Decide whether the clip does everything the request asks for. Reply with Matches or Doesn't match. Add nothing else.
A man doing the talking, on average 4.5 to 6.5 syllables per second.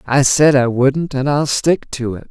Doesn't match